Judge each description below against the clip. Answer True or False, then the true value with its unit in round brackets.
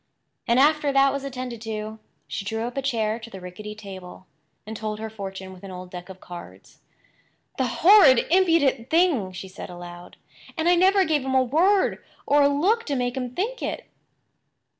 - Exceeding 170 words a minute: True (190 wpm)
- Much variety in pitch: True (6.9 semitones)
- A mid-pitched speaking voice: False (235 Hz)